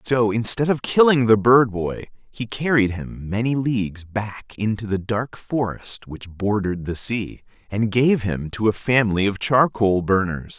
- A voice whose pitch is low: Yes, low, 110 Hz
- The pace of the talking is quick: No, average, 170 wpm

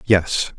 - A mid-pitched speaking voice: No, very low, 95 Hz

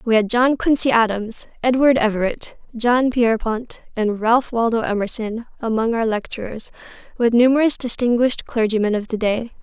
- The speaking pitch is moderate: No, high, 230 Hz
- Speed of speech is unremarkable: Yes, average, 145 wpm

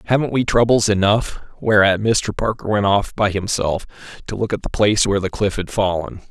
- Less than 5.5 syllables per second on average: No, 5.6 syllables/s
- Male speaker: Yes, male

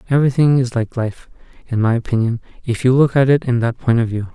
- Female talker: No, male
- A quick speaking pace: Yes, fast, 235 wpm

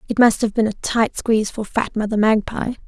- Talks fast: Yes, fast, 230 wpm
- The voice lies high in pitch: Yes, high, 220 Hz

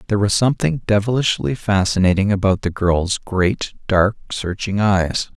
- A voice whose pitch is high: No, low, 100 Hz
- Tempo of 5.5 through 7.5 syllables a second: No, 4.7 syllables/s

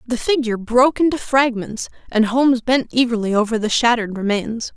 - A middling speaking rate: Yes, average, 165 wpm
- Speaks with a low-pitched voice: No, high, 235 Hz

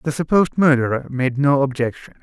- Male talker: Yes, male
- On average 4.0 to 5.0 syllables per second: No, 5.7 syllables/s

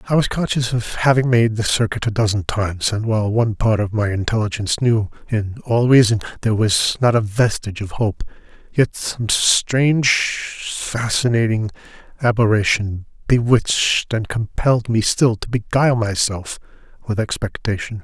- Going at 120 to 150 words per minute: Yes, average, 145 wpm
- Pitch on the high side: No, low, 110 Hz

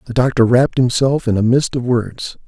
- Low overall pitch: Yes, low, 120 Hz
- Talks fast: Yes, fast, 220 wpm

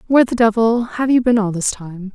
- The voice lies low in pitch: No, high, 220 Hz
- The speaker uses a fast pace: Yes, fast, 250 wpm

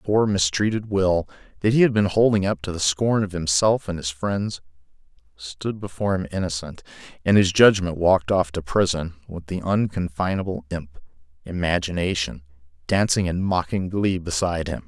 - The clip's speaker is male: Yes, male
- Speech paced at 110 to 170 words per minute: Yes, average, 160 wpm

